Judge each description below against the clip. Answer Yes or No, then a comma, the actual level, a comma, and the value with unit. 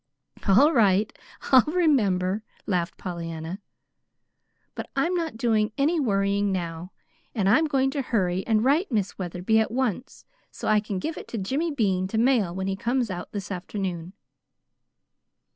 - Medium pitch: No, high, 210 Hz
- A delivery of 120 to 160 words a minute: Yes, average, 155 wpm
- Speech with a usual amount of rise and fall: No, wide, 5.8 semitones